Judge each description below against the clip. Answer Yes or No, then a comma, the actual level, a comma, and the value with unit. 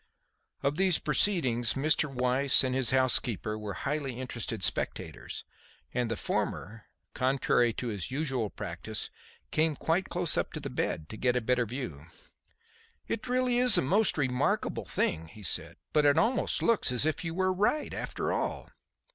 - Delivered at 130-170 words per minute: Yes, average, 165 wpm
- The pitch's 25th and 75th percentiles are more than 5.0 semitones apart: Yes, wide, 5.4 semitones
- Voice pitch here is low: Yes, low, 130 Hz